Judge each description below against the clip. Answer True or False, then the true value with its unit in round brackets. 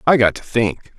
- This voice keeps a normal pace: False (245 wpm)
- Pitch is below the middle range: True (120 Hz)